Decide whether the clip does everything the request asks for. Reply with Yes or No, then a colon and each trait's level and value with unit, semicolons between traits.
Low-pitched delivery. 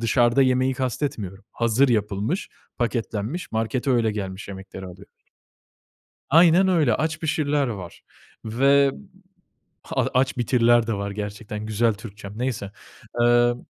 Yes: low, 120 Hz